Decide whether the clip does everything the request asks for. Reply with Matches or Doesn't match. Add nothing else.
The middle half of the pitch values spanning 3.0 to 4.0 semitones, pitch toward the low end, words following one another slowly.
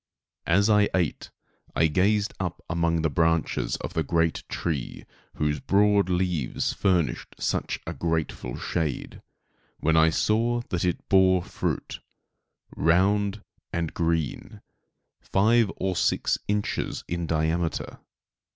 Matches